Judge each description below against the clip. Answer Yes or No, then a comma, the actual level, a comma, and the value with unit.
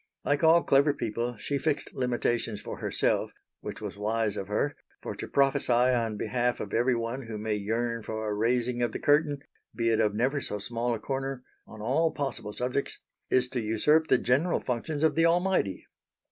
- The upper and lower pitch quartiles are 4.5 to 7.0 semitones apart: No, average, 4.0 semitones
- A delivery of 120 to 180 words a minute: No, average, 190 wpm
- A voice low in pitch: Yes, low, 120 Hz